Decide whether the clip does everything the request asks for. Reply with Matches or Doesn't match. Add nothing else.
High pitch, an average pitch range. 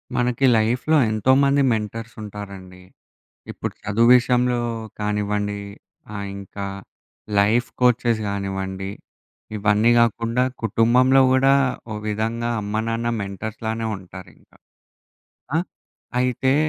Doesn't match